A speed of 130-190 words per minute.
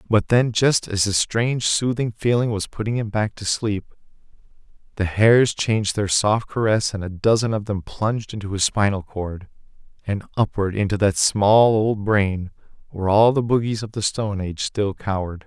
Yes: average, 180 wpm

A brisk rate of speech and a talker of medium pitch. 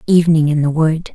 Yes: fast, 210 wpm; medium, 160 Hz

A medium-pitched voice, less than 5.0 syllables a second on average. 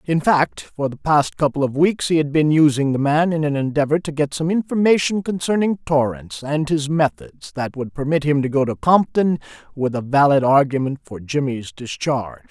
No: medium, 145 Hz; 5.1 syllables/s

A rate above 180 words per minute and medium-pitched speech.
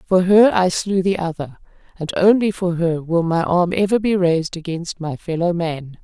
Yes: average, 200 wpm; medium, 175 Hz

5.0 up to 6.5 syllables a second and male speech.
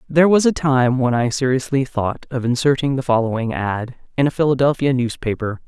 No: 5.6 syllables/s; female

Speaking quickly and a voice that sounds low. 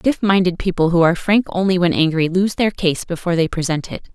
No: fast, 230 wpm; medium, 180 Hz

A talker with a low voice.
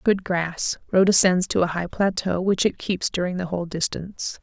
No: medium, 180 Hz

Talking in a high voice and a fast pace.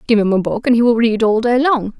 Yes: high, 230 Hz; fast, 330 wpm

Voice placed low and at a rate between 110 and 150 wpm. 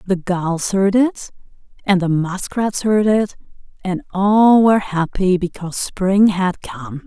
No: high, 190 Hz; average, 145 wpm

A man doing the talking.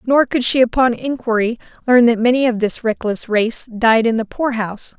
No: female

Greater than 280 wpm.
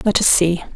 No: fast, 240 wpm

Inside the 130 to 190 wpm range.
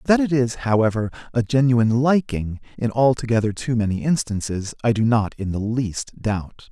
Yes: average, 170 wpm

